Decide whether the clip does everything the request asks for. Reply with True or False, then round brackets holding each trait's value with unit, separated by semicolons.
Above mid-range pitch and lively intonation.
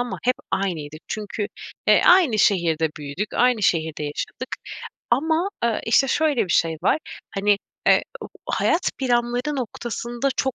True (235 Hz; 6.9 semitones)